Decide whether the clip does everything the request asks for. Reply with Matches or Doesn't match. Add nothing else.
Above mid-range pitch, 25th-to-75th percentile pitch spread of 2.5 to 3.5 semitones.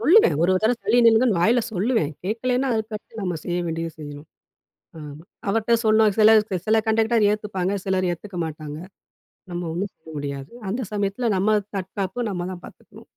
Doesn't match